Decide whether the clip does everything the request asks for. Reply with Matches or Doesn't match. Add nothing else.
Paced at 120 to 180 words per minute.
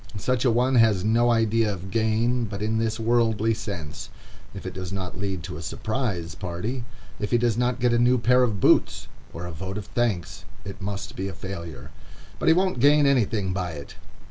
Doesn't match